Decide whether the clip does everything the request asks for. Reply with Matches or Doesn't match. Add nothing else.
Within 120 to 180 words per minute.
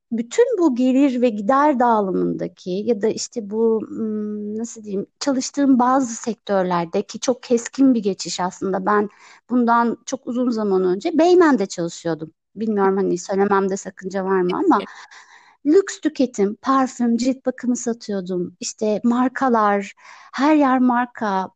Matches